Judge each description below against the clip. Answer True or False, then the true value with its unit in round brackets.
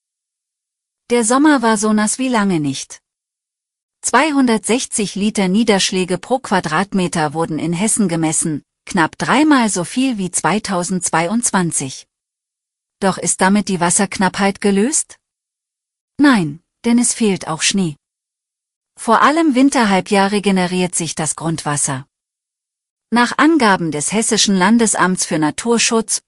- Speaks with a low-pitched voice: False (195 Hz)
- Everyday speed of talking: False (110 wpm)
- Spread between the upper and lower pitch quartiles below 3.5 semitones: False (5.3 semitones)